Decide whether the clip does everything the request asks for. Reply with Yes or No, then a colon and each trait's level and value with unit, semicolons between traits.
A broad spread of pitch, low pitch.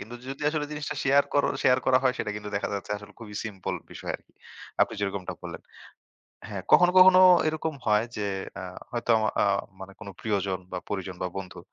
Yes: wide, 5.7 semitones; low, 110 Hz